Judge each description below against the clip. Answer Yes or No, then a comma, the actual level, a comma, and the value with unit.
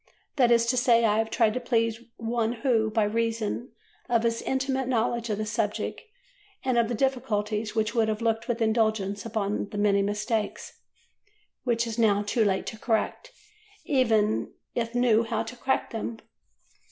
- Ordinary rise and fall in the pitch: No, narrow, 1.8 semitones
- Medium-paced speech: Yes, average, 170 wpm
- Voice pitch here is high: Yes, high, 225 Hz